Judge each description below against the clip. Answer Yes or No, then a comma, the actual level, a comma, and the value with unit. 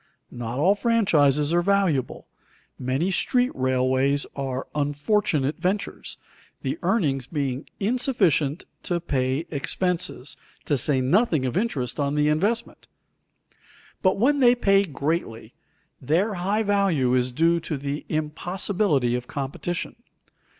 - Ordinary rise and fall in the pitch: No, wide, 6.4 semitones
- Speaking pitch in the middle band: Yes, medium, 155 Hz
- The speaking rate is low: Yes, slow, 120 wpm